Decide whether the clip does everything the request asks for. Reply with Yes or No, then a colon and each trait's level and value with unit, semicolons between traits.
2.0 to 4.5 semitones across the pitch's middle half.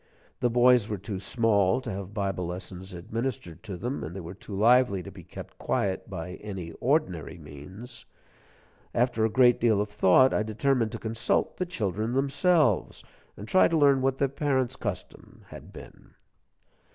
No: average, 5.2 semitones